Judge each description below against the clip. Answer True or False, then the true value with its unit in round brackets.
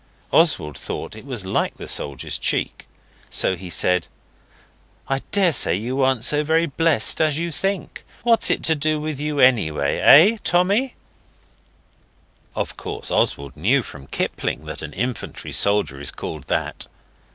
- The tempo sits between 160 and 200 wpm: False (150 wpm)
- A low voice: True (130 Hz)